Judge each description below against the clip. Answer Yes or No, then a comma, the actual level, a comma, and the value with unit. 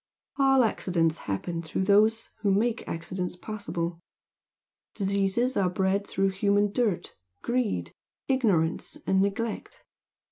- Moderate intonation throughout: Yes, average, 3.5 semitones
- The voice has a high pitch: Yes, high, 200 Hz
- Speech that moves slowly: Yes, slow, 110 wpm